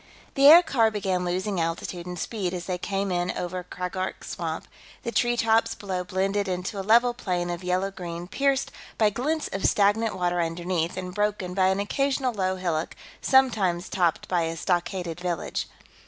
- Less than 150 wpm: No, average, 170 wpm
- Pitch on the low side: No, medium, 185 Hz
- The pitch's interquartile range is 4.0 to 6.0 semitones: No, average, 3.1 semitones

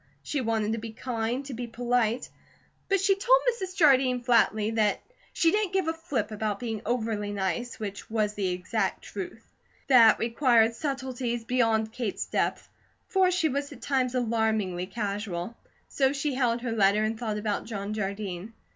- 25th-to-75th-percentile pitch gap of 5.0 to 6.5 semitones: No, average, 3.5 semitones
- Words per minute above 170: No, average, 165 wpm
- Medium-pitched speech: No, high, 230 Hz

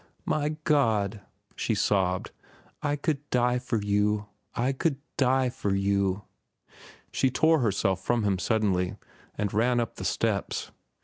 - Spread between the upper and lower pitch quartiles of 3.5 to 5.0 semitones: Yes, average, 4.7 semitones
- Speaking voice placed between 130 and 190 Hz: No, low, 110 Hz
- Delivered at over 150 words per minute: No, slow, 135 wpm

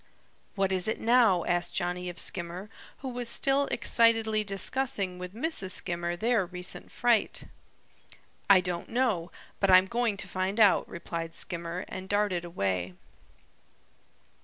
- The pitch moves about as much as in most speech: Yes, average, 4.3 semitones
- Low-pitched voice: No, high, 190 Hz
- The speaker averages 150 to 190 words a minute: No, slow, 135 wpm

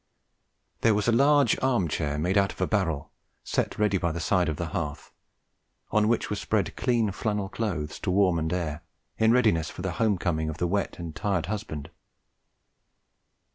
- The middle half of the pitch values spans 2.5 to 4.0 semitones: No, average, 4.7 semitones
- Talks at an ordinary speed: Yes, average, 185 wpm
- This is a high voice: No, very low, 95 Hz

